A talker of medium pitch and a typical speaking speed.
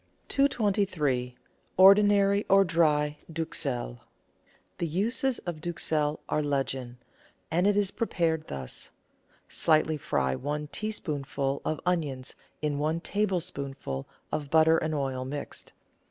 No: medium, 155 Hz; slow, 115 wpm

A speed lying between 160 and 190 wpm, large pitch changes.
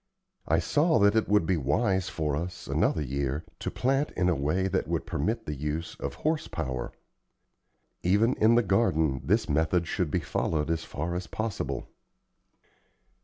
Yes: average, 170 wpm; wide, 6.1 semitones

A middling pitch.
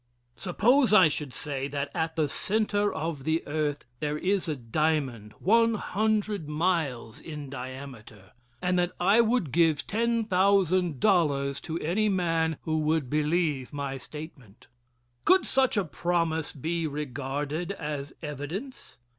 Yes: medium, 160 Hz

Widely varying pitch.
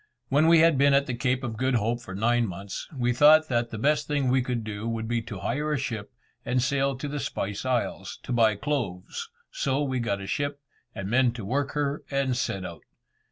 No: average, 3.9 semitones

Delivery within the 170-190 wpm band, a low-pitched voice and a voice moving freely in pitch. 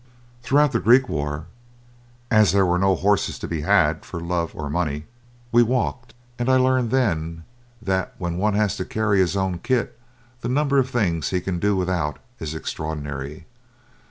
Yes: average, 175 wpm; very low, 95 Hz; wide, 6.3 semitones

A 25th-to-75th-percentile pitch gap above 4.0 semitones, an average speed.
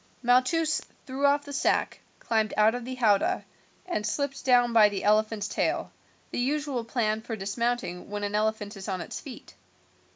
No: average, 3.6 semitones; average, 170 wpm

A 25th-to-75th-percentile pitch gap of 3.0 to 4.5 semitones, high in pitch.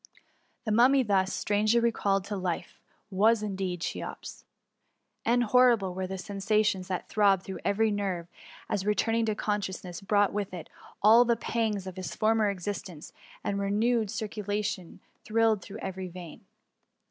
No: narrow, 2.5 semitones; high, 205 Hz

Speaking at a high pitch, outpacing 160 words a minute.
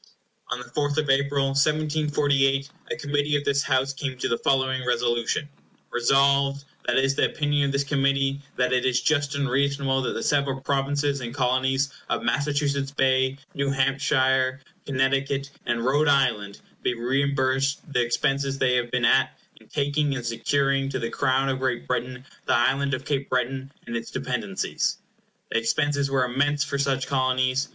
No: low, 135 Hz; average, 170 wpm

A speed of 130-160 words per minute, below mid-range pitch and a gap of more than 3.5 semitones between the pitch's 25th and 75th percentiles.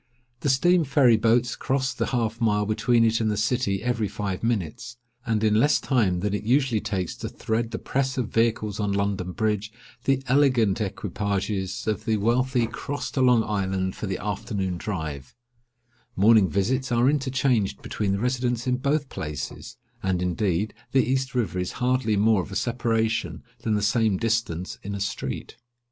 No: average, 170 wpm; low, 110 Hz; average, 3.9 semitones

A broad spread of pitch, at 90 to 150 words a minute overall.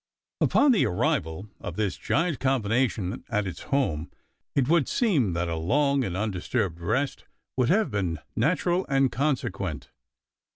Yes: wide, 7.8 semitones; average, 140 wpm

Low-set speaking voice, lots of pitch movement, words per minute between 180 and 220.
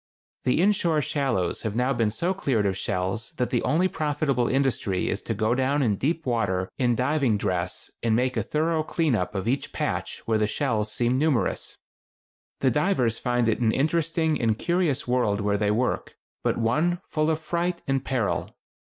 Yes: low, 125 Hz; wide, 5.8 semitones; average, 185 wpm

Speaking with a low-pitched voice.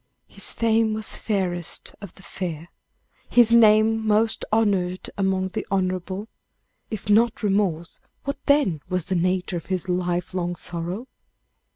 No: high, 190 Hz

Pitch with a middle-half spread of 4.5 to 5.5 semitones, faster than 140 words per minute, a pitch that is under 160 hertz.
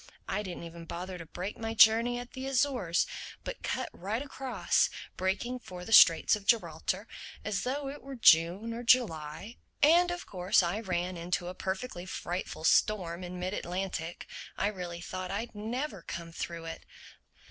No: average, 5.1 semitones; average, 165 wpm; high, 190 Hz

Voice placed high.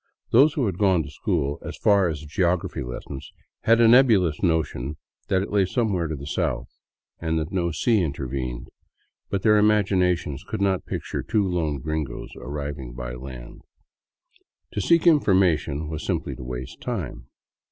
No: very low, 85 Hz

